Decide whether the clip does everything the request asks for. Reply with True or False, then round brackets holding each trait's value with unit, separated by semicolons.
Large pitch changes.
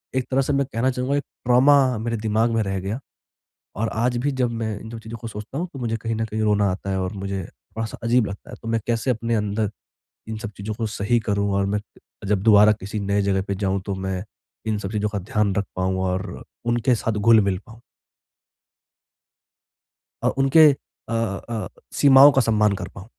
False (2.8 semitones)